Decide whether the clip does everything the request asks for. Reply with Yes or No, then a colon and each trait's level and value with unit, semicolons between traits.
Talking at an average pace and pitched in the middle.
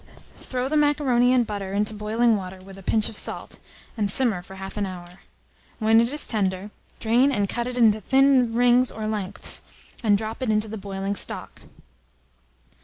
No: average, 180 wpm; high, 215 Hz